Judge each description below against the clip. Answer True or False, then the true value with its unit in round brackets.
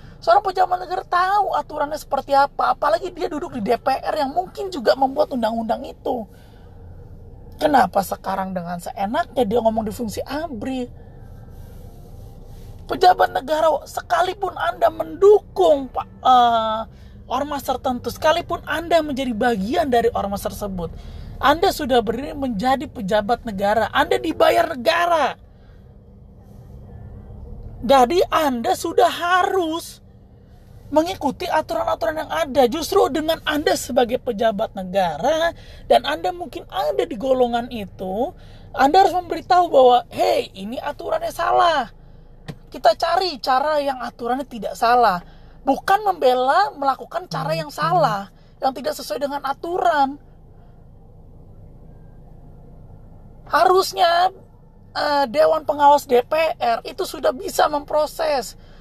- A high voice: True (280 Hz)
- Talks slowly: False (110 wpm)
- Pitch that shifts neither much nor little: False (6.2 semitones)